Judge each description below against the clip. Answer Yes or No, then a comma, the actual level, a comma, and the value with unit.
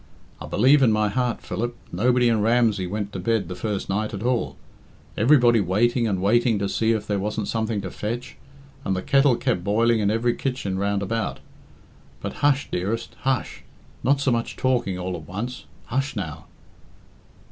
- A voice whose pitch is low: Yes, low, 110 Hz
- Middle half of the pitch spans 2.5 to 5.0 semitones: Yes, average, 3.4 semitones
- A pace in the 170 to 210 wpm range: Yes, average, 180 wpm